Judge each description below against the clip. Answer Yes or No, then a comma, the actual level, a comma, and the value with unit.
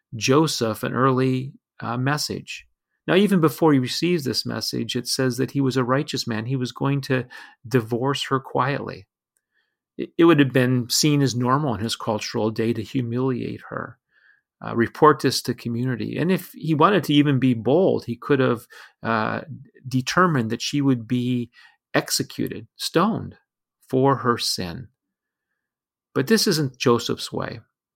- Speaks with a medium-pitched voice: No, low, 130 Hz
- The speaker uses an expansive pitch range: No, average, 3.2 semitones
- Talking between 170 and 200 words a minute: No, average, 155 wpm